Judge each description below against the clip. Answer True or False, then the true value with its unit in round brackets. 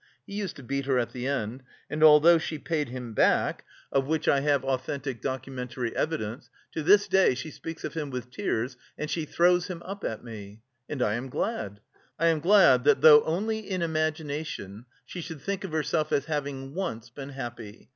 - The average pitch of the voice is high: False (145 Hz)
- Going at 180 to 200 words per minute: True (195 wpm)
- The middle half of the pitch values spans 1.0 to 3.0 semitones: False (4.5 semitones)